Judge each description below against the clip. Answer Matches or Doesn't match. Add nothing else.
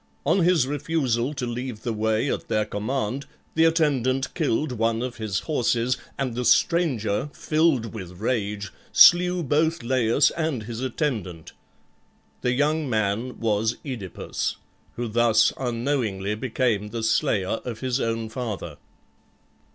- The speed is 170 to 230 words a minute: Doesn't match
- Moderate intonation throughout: Matches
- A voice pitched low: Matches